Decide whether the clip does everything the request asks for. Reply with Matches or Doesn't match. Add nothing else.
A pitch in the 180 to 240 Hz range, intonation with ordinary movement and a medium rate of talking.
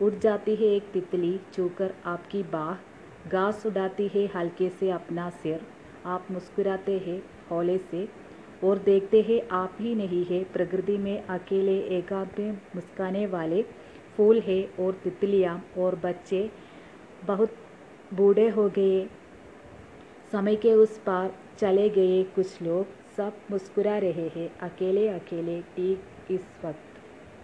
Doesn't match